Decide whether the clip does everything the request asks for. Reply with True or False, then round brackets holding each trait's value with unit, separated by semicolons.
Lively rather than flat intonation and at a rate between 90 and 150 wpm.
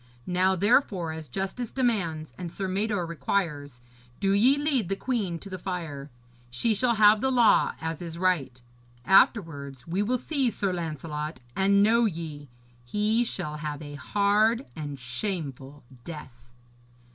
True (5.7 semitones; 145 wpm)